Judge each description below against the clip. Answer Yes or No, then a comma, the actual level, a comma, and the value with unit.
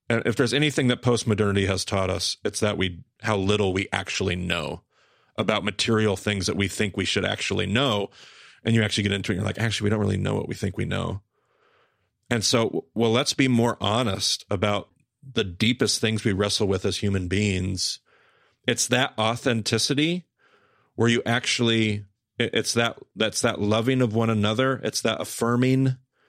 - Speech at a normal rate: Yes, average, 185 wpm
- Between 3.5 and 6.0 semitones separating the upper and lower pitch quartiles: No, average, 2.7 semitones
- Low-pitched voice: Yes, low, 110 Hz